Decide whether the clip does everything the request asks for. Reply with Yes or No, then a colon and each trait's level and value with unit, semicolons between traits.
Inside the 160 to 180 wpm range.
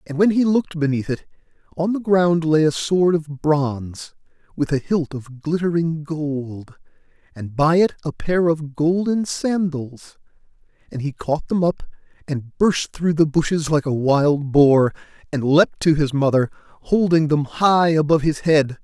Yes: average, 170 wpm